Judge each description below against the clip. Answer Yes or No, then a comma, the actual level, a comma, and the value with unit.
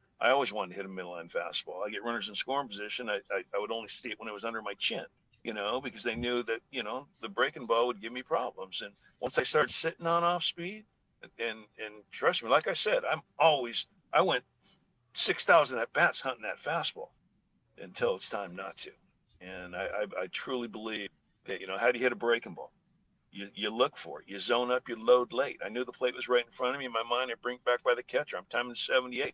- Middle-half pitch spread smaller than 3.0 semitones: Yes, narrow, 2.6 semitones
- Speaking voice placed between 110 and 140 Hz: Yes, low, 120 Hz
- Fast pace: Yes, fast, 255 wpm